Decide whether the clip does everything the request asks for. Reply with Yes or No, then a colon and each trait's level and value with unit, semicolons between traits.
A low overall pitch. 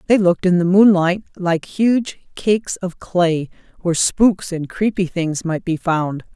No: medium, 180 Hz